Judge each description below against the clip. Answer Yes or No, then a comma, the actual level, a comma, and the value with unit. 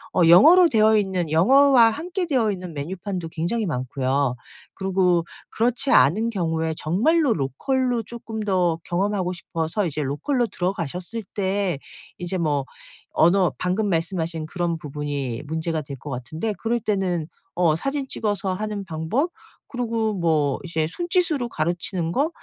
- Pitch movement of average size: No, wide, 5.7 semitones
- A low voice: No, medium, 185 Hz